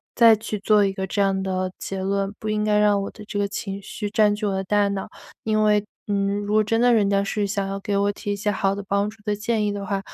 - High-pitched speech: Yes, high, 205 Hz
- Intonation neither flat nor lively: No, narrow, 1.2 semitones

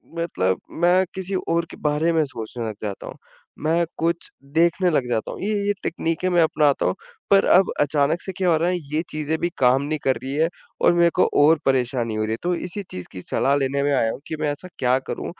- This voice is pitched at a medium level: Yes, medium, 155 Hz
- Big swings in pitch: No, average, 4.5 semitones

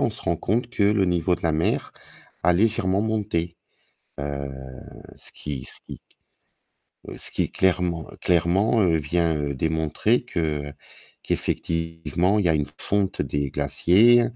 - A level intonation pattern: No, average, 3.9 semitones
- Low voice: Yes, very low, 85 Hz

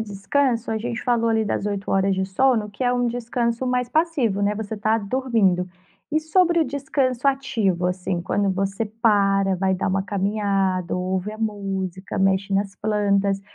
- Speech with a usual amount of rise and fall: Yes, average, 3.7 semitones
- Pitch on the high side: Yes, high, 205 Hz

